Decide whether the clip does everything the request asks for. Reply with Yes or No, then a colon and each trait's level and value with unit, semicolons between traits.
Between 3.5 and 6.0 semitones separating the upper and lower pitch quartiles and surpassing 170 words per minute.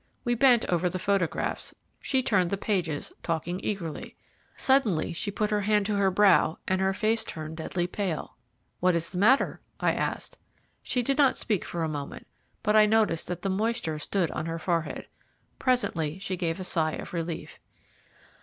Yes: average, 4.4 semitones; average, 180 wpm